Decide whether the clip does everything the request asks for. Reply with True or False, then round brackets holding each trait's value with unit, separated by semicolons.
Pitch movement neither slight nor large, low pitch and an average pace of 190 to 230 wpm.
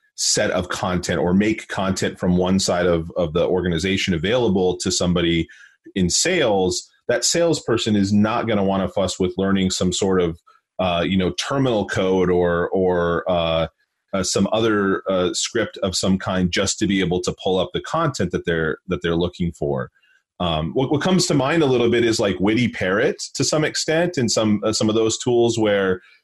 True (4.1 semitones; 95 Hz; 200 wpm)